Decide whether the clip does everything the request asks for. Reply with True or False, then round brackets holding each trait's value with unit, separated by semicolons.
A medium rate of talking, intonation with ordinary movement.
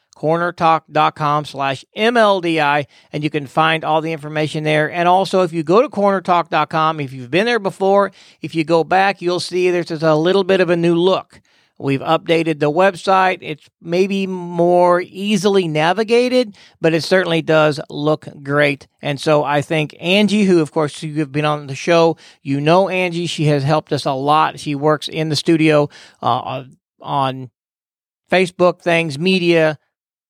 True (170 wpm; 3.1 semitones)